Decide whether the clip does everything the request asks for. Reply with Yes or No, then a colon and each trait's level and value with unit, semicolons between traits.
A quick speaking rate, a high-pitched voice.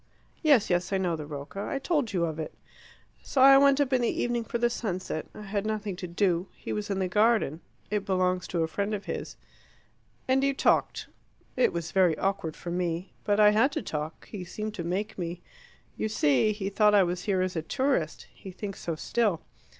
Yes: fast, 215 wpm; high, 195 Hz